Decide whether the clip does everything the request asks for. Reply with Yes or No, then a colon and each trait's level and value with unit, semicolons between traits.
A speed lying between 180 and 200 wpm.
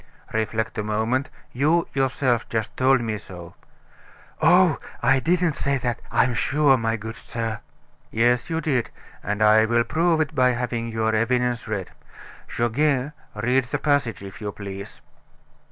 No: average, 150 wpm